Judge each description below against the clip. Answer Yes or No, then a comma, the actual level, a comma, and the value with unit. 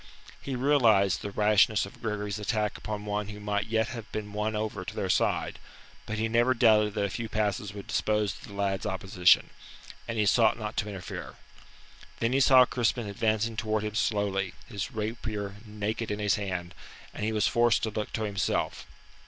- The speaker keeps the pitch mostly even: Yes, narrow, 1.6 semitones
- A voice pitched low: Yes, low, 105 Hz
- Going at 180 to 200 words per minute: Yes, average, 190 wpm